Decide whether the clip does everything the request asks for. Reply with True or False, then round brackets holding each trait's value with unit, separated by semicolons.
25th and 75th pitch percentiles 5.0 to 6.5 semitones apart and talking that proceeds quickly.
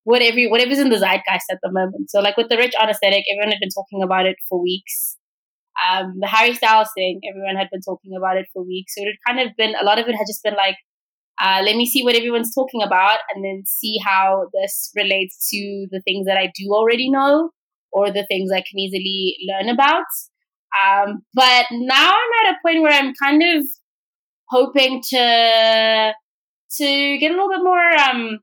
True (5.3 semitones; 210 wpm)